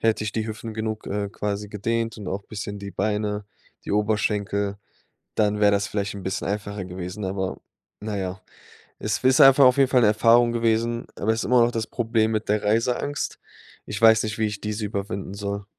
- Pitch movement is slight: Yes, narrow, 1.9 semitones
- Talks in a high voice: No, low, 105 Hz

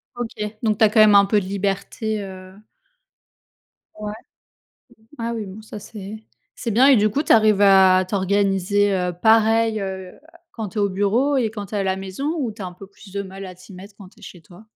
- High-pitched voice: Yes, high, 205 Hz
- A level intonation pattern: Yes, narrow, 2.3 semitones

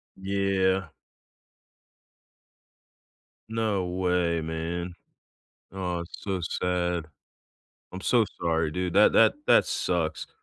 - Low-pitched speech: Yes, very low, 90 Hz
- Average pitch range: No, narrow, 2.0 semitones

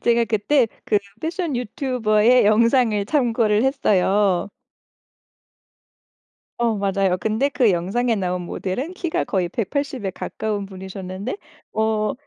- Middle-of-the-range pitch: No, high, 220 Hz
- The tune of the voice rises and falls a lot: No, average, 4.1 semitones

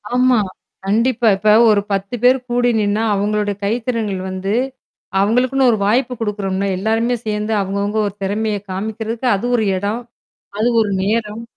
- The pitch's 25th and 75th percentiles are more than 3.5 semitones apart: No, narrow, 2.6 semitones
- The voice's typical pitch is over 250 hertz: No, high, 215 Hz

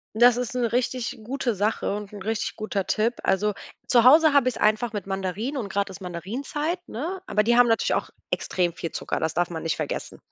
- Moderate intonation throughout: Yes, average, 4.2 semitones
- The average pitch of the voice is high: Yes, high, 220 Hz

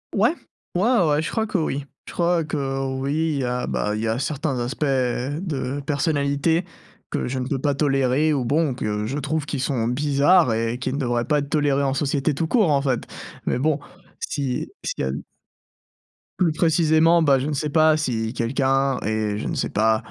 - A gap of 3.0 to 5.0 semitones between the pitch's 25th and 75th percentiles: Yes, average, 3.6 semitones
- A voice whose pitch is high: No, medium, 140 Hz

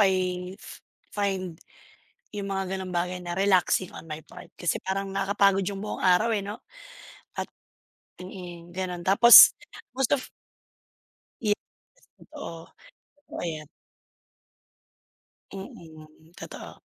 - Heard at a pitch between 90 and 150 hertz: No, high, 190 Hz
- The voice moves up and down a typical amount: No, narrow, 2.2 semitones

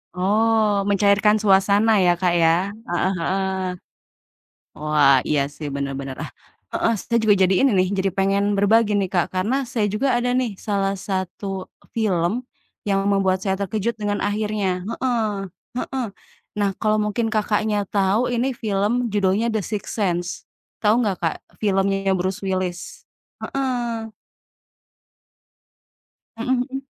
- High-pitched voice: Yes, high, 200 Hz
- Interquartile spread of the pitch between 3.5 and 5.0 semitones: No, average, 2.7 semitones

